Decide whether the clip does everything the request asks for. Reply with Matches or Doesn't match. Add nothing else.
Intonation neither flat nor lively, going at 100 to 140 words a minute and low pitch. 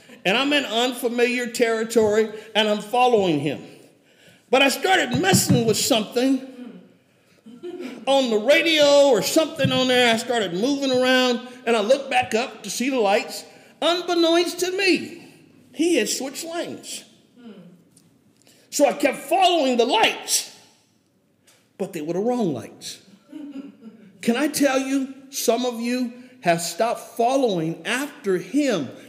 Doesn't match